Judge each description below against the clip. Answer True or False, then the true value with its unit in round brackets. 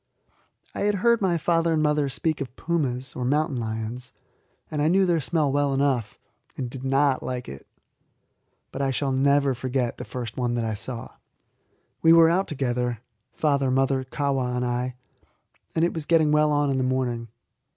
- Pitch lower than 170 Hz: True (135 Hz)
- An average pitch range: True (3.6 semitones)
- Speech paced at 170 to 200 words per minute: True (180 wpm)